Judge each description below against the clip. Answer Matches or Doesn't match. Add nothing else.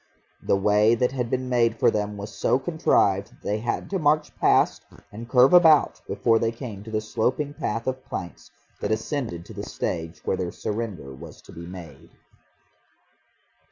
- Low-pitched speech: Matches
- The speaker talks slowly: Doesn't match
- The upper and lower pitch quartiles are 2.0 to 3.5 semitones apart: Doesn't match